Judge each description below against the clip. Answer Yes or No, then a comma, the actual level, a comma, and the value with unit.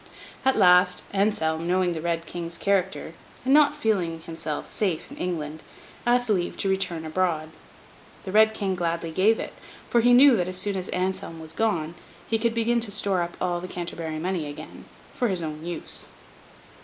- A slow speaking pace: No, average, 180 wpm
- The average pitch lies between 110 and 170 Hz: No, medium, 180 Hz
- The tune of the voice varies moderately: Yes, average, 4.0 semitones